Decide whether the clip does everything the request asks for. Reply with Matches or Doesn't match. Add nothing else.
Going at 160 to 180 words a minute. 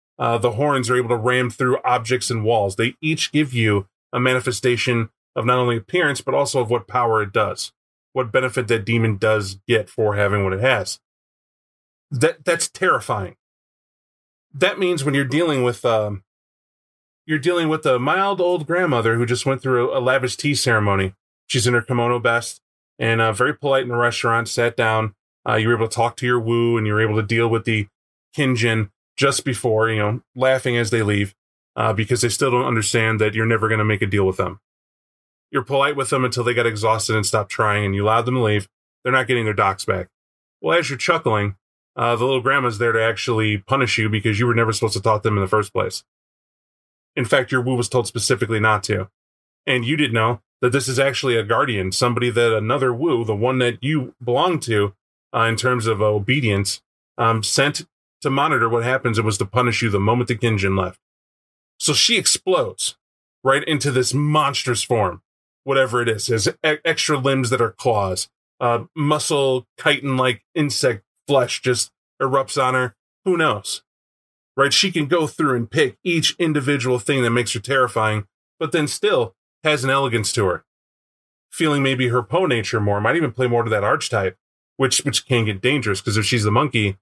Doesn't match